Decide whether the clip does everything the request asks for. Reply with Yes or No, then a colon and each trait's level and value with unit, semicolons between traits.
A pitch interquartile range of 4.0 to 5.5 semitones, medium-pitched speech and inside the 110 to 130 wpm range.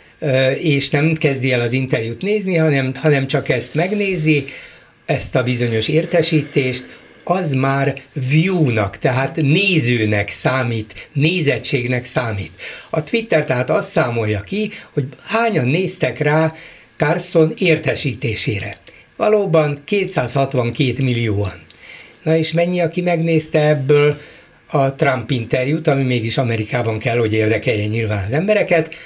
Yes: average, 4.4 semitones; medium, 145 Hz; average, 120 wpm